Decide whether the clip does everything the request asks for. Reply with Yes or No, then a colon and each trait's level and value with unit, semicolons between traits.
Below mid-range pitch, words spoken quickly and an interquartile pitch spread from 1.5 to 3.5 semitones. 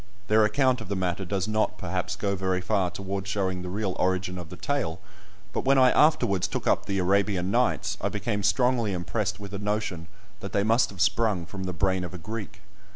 Yes: low, 100 Hz; fast, 215 wpm; narrow, 2.6 semitones